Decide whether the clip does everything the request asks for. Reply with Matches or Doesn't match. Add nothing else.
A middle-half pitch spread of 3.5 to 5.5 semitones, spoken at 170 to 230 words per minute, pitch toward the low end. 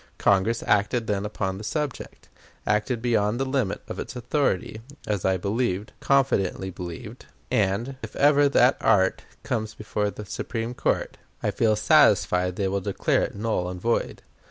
Doesn't match